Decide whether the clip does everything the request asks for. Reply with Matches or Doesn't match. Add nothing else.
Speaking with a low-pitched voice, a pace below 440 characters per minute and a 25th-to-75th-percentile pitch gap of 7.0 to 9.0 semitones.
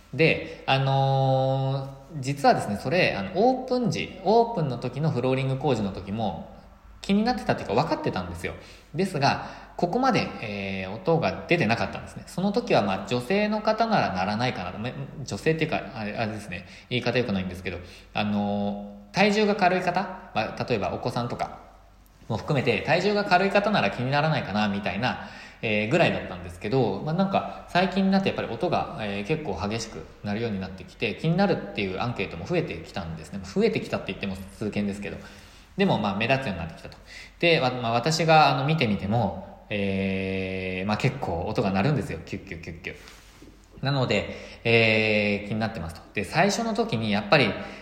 Matches